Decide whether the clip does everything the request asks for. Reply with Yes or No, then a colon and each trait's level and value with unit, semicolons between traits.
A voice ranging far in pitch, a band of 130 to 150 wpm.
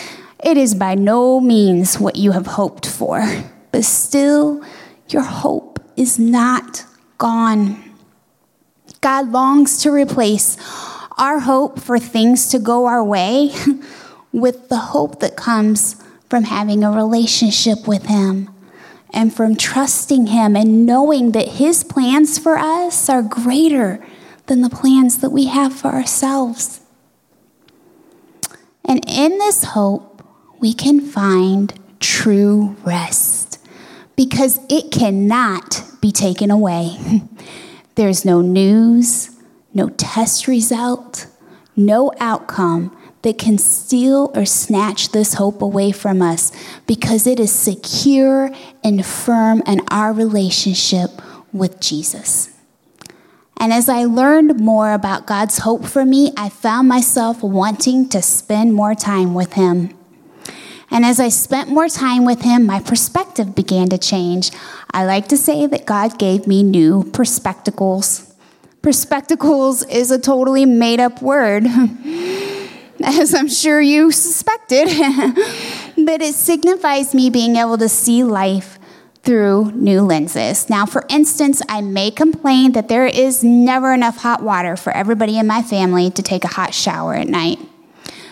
No: average, 4.9 semitones; slow, 135 wpm